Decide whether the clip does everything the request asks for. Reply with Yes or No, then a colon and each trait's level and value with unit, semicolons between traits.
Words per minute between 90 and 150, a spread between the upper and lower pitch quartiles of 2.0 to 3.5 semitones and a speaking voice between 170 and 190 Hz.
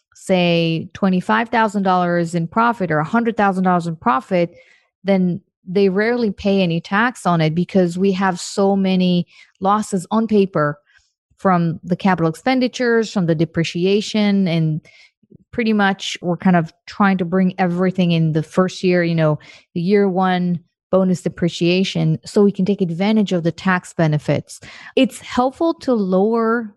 Yes: average, 145 wpm; average, 2.9 semitones; medium, 185 Hz